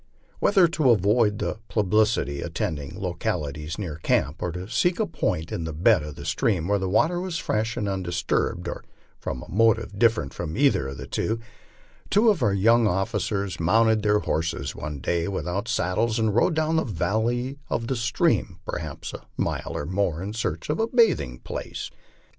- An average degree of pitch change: No, wide, 5.7 semitones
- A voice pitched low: Yes, low, 105 Hz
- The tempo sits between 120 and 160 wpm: No, average, 180 wpm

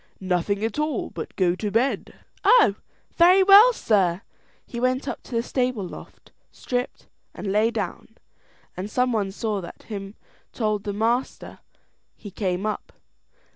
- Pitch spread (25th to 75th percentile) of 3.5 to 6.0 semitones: Yes, average, 4.2 semitones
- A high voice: Yes, high, 220 Hz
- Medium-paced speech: Yes, average, 155 wpm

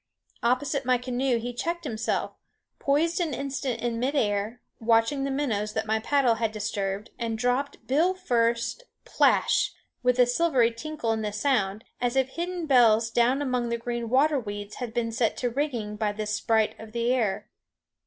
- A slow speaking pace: No, average, 175 wpm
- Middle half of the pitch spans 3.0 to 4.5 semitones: Yes, average, 3.6 semitones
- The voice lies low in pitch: No, high, 240 Hz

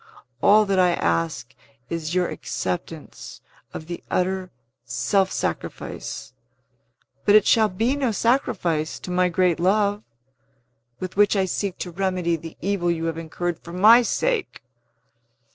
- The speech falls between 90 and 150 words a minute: Yes, average, 140 wpm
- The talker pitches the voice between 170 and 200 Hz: Yes, medium, 185 Hz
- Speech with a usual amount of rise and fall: Yes, average, 3.3 semitones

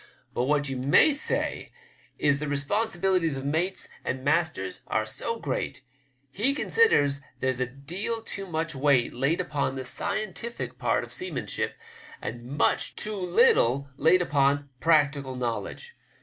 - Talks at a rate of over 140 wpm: Yes, average, 150 wpm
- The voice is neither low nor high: Yes, medium, 145 Hz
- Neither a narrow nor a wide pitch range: No, wide, 5.9 semitones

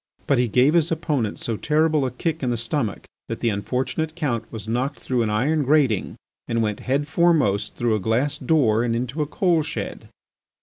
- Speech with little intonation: No, average, 5.0 semitones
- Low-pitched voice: Yes, low, 130 Hz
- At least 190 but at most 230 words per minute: Yes, average, 200 wpm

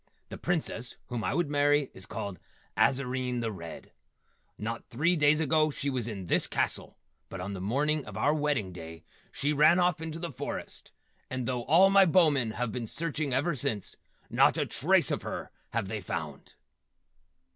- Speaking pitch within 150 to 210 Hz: No, low, 135 Hz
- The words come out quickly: No, average, 180 wpm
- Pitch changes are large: Yes, wide, 5.7 semitones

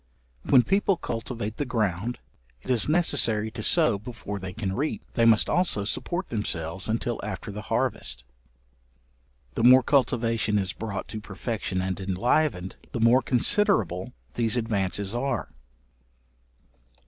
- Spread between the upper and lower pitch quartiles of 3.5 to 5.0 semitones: Yes, average, 4.1 semitones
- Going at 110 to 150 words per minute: Yes, slow, 135 wpm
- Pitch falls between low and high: No, low, 115 Hz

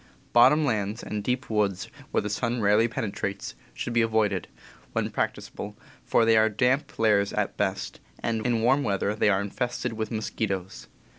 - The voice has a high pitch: No, low, 110 Hz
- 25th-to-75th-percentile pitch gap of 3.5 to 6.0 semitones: No, average, 2.7 semitones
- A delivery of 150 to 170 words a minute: Yes, average, 165 wpm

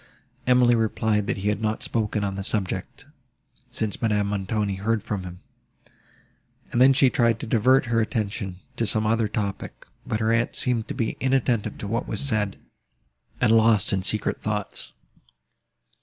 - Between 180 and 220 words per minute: No, average, 160 wpm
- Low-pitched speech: Yes, low, 110 Hz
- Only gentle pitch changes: Yes, narrow, 2.2 semitones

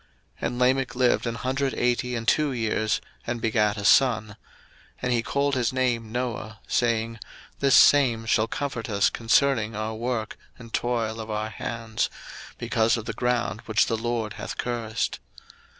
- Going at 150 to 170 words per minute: Yes, average, 165 wpm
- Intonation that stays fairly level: Yes, narrow, 2.0 semitones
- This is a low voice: Yes, low, 115 Hz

